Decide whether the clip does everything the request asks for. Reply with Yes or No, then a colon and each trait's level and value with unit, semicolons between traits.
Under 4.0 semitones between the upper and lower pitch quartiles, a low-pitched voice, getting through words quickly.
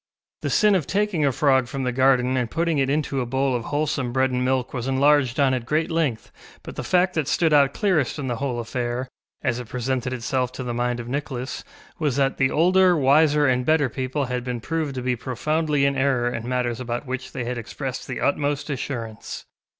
Yes: average, 2.9 semitones; low, 130 Hz; fast, 220 wpm